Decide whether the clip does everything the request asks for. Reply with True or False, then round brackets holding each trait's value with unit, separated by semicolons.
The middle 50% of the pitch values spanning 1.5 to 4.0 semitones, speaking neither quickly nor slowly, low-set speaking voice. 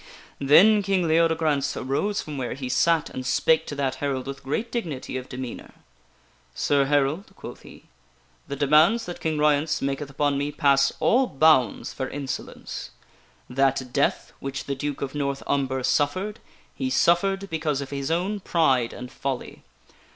False (3.3 semitones; 165 wpm; 145 Hz)